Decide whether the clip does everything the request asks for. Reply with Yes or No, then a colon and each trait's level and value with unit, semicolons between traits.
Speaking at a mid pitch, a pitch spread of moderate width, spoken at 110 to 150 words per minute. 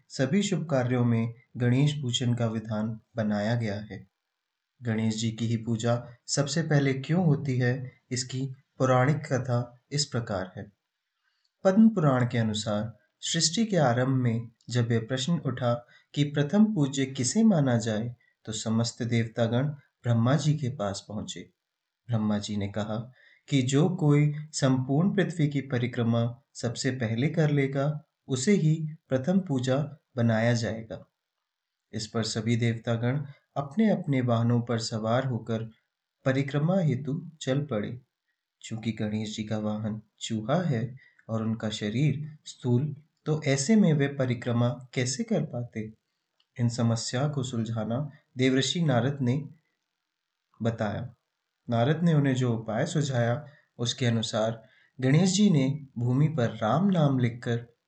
No: low, 125 Hz; average, 4.1 semitones; average, 135 wpm